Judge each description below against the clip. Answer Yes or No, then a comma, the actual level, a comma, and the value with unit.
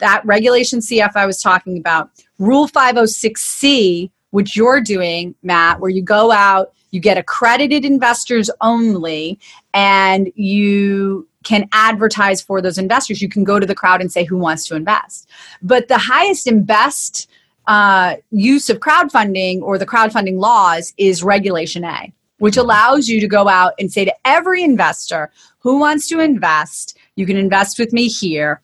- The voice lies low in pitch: No, high, 200 Hz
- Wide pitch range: No, average, 3.7 semitones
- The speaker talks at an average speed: Yes, average, 165 wpm